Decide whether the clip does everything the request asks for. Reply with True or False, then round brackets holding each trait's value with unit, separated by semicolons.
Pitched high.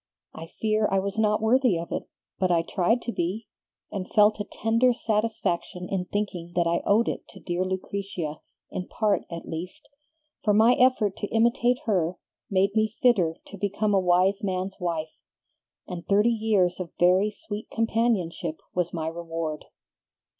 True (195 Hz)